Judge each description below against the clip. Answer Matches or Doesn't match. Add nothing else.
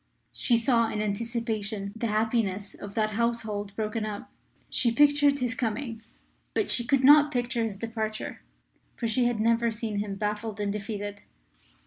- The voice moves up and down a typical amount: Doesn't match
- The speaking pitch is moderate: Doesn't match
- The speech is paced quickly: Doesn't match